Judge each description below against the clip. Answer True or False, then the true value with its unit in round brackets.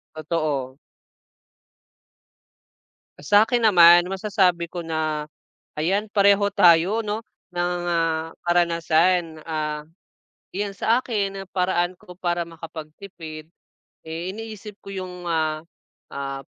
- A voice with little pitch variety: False (3.7 semitones)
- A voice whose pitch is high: False (175 Hz)